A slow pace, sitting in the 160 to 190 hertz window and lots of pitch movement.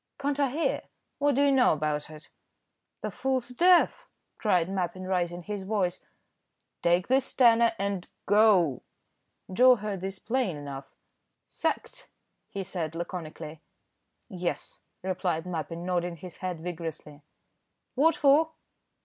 Yes: slow, 125 wpm; medium, 185 Hz; wide, 6.6 semitones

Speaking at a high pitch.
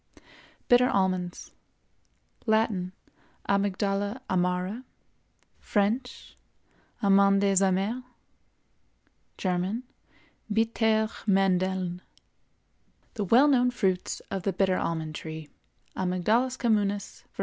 Yes: high, 195 Hz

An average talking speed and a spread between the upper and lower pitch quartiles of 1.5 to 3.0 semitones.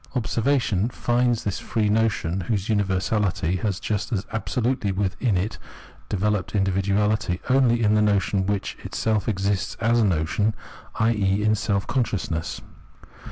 No: slow, 125 wpm; narrow, 2.6 semitones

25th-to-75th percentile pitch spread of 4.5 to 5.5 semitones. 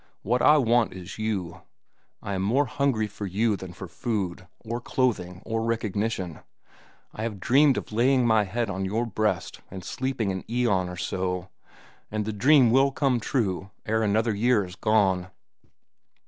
No: average, 4.1 semitones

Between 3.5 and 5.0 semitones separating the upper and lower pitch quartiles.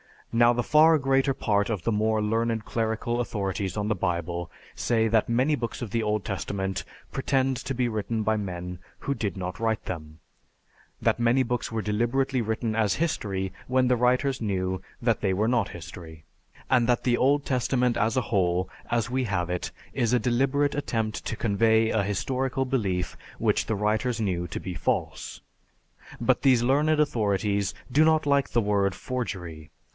Yes: average, 4.2 semitones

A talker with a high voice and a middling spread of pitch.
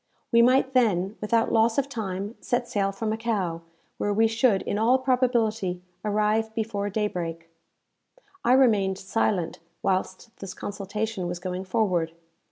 Yes: high, 210 Hz; average, 3.2 semitones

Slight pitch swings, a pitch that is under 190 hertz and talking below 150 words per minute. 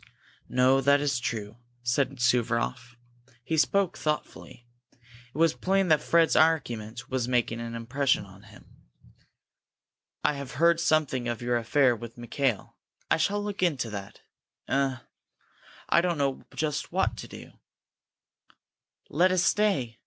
No: average, 4.8 semitones; low, 135 Hz; average, 140 wpm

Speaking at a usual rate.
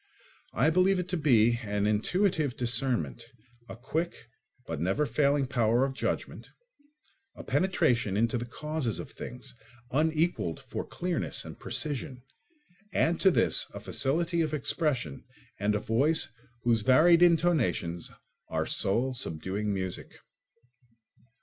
No: slow, 125 wpm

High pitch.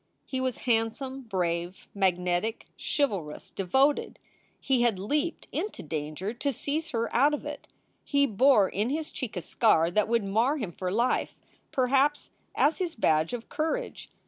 Yes: high, 235 Hz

